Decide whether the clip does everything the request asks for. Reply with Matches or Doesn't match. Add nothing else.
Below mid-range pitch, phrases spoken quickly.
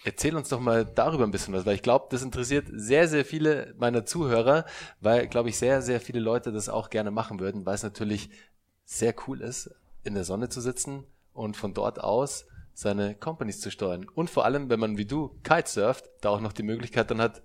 Matches